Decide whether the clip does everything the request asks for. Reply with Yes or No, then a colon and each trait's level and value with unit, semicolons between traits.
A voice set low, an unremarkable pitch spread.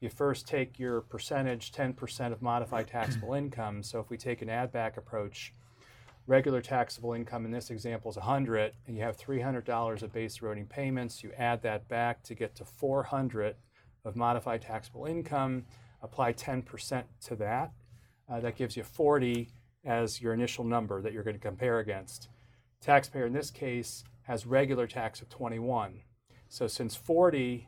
No: low, 120 Hz; narrow, 1.8 semitones